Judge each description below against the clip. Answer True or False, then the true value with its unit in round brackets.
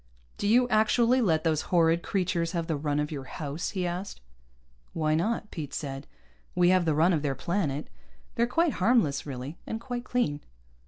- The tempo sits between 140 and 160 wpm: False (180 wpm)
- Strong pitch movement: True (5.9 semitones)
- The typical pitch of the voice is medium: True (170 Hz)